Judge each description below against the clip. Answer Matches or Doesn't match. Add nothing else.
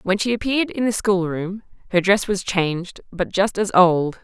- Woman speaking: Matches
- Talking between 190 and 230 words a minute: Matches